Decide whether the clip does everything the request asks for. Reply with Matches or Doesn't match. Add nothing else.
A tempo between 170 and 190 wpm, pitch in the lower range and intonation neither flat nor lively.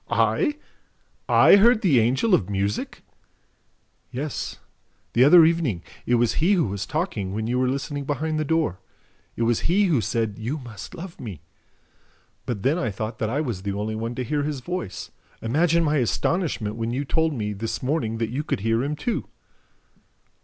Doesn't match